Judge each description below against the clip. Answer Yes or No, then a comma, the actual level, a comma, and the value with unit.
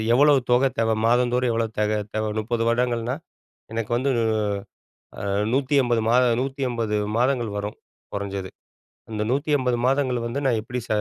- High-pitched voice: No, low, 120 Hz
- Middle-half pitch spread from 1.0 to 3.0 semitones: Yes, narrow, 2.6 semitones